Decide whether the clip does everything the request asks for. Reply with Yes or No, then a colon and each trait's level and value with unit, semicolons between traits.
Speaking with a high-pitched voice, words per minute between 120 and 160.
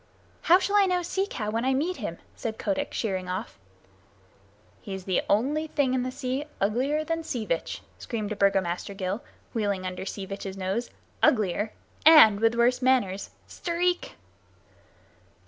Yes: high, 230 Hz; average, 155 wpm